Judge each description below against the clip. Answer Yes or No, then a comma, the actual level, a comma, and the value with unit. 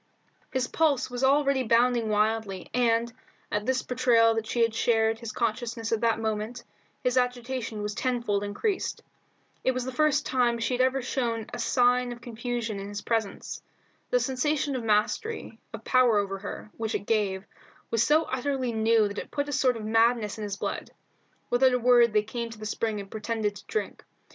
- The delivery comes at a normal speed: Yes, average, 190 wpm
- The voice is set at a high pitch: Yes, high, 235 Hz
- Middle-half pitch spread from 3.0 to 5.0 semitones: No, narrow, 2.6 semitones